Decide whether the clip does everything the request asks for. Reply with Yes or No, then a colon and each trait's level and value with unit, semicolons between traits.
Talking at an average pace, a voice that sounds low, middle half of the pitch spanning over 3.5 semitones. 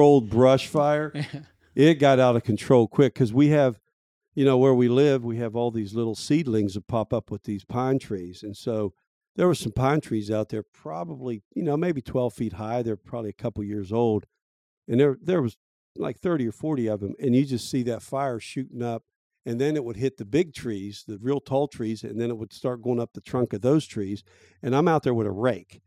No: fast, 235 wpm; low, 120 Hz; average, 4.0 semitones